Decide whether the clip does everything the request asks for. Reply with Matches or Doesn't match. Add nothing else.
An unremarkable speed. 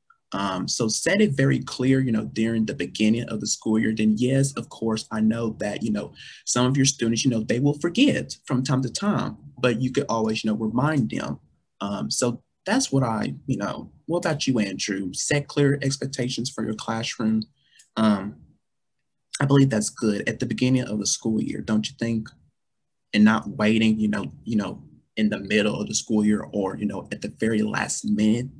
Doesn't match